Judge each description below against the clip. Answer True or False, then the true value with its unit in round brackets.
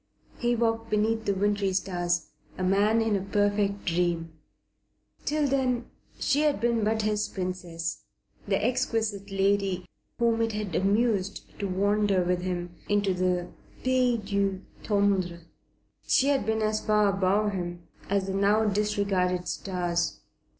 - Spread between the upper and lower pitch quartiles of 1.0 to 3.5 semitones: True (3.0 semitones)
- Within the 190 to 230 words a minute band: False (140 wpm)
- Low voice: False (200 Hz)